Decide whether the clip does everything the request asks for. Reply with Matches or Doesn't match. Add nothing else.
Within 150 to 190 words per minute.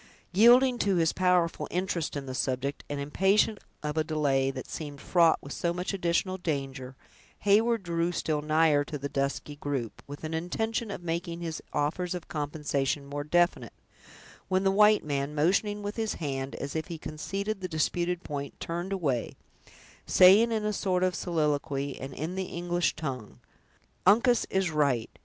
Matches